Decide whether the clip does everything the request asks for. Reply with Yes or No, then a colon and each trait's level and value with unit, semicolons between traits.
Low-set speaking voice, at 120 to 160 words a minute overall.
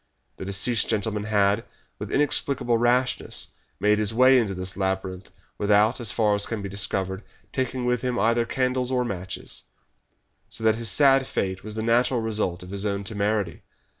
No: low, 110 Hz; average, 170 wpm